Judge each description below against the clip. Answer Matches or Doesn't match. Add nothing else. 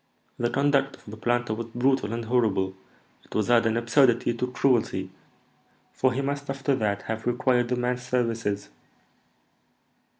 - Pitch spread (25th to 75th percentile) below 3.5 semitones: Matches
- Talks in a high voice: Doesn't match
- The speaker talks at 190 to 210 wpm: Doesn't match